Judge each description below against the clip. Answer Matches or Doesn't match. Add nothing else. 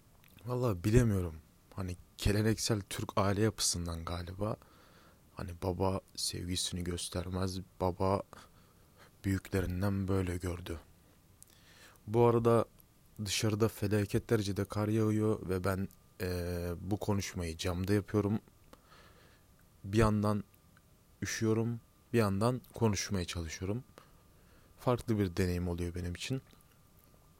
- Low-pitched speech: Matches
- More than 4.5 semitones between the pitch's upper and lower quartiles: Doesn't match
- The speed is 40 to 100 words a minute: Matches